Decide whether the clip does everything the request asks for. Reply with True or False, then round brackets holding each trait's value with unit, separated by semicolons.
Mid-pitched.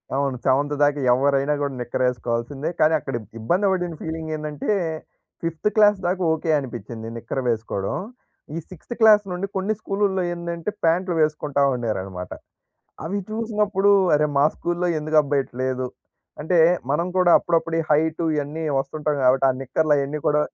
True (150 Hz)